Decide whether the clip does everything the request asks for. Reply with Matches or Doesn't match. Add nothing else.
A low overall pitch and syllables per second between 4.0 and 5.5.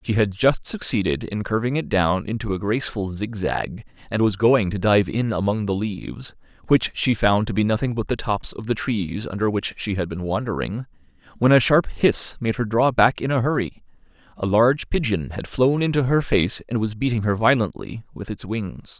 Matches